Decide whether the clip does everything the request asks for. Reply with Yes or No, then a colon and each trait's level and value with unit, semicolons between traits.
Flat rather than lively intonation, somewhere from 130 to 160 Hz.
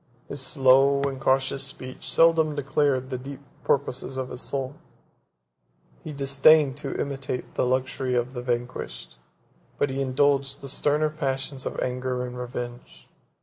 Yes: narrow, 1.6 semitones; low, 135 Hz